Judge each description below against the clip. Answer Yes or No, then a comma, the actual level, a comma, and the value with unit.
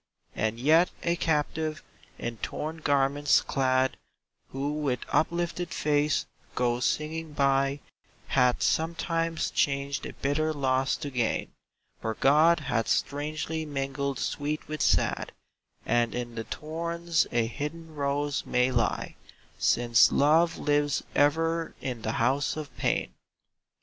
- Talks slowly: Yes, slow, 125 wpm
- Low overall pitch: No, medium, 145 Hz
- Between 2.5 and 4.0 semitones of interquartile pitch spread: Yes, average, 3.2 semitones